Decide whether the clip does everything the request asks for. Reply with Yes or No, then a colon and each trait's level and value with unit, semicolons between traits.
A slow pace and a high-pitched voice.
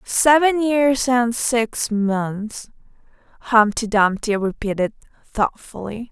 Yes: slow, 90 wpm; high, 230 Hz